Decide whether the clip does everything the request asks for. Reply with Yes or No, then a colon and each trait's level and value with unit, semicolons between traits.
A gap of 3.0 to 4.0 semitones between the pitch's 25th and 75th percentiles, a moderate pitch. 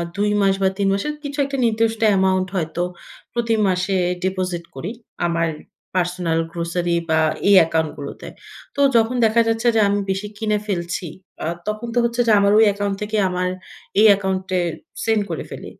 No: average, 3.5 semitones; high, 195 Hz